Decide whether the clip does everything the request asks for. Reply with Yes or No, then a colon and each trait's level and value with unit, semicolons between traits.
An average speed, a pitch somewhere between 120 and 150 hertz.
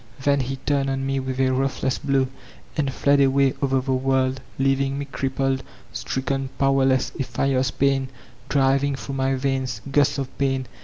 Yes: average, 170 wpm; low, 135 Hz